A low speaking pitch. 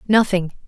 No: high, 195 Hz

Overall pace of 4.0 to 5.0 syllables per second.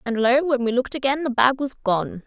No: 5.6 syllables/s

